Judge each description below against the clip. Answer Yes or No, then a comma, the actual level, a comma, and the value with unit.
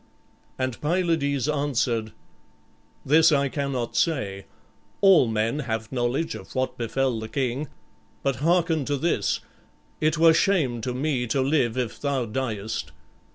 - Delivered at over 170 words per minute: No, slow, 135 wpm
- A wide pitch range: No, average, 4.4 semitones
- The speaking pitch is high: No, low, 135 Hz